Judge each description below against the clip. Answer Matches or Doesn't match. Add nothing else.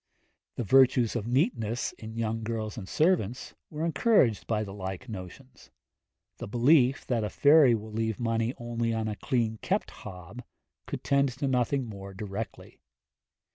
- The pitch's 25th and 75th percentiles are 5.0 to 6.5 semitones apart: Doesn't match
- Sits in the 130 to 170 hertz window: Doesn't match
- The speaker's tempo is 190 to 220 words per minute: Doesn't match